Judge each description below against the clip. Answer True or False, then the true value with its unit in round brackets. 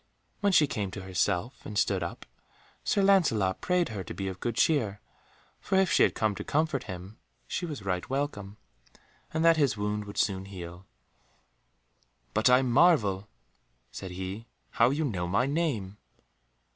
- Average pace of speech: True (165 wpm)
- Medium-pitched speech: False (110 Hz)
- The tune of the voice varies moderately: False (7.2 semitones)